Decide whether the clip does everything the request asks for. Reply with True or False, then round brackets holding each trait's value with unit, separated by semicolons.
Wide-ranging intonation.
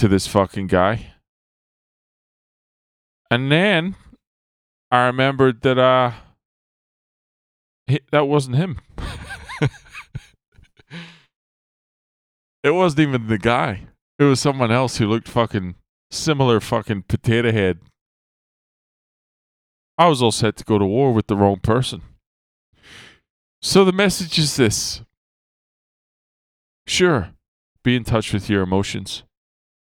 True (6.0 semitones)